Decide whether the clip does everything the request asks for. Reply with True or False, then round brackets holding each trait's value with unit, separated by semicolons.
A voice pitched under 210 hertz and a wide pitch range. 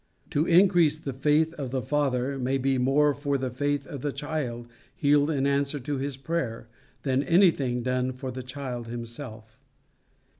False (135 Hz; 2.5 semitones)